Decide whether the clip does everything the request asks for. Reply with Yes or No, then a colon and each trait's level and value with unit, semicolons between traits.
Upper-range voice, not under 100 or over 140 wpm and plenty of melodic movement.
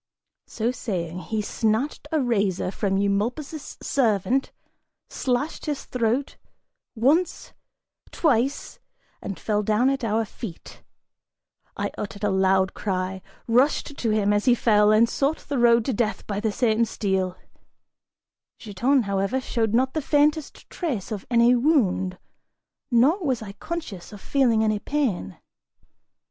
No: high, 225 Hz; slow, 135 wpm; average, 4.7 semitones